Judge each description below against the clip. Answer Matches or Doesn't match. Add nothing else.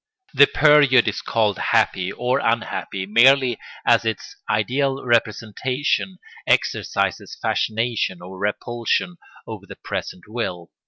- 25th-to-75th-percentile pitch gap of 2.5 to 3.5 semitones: Doesn't match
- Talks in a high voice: Doesn't match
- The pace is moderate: Doesn't match